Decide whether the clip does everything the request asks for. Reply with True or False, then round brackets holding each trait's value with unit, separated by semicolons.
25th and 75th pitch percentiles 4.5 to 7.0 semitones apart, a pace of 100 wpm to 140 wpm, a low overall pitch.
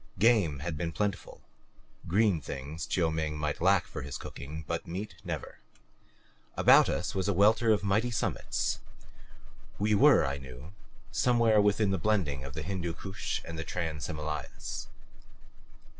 False (5.2 semitones; 150 wpm; 85 Hz)